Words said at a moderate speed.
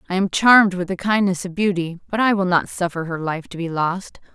No: fast, 250 wpm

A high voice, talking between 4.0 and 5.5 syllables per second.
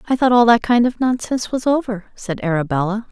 No: high, 225 Hz; 6.0 syllables/s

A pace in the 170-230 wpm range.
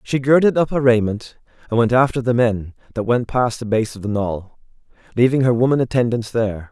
Yes: fast, 205 wpm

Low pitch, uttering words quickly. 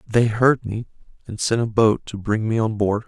Yes: low, 110 Hz; fast, 235 wpm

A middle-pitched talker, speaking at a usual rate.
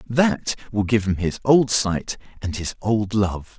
No: low, 105 Hz; average, 185 wpm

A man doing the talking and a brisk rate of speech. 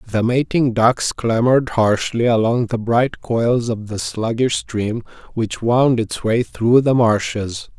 No: male; average, 155 wpm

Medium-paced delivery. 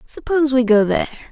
Yes: average, 185 wpm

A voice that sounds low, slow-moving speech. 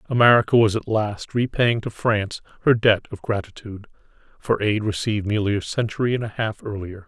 No: low, 105 Hz; average, 180 wpm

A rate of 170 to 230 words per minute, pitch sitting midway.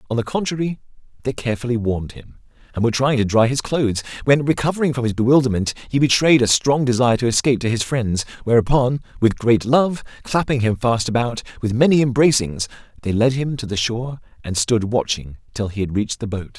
No: average, 200 wpm; low, 120 Hz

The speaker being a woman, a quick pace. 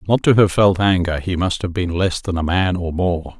No: male; fast, 265 wpm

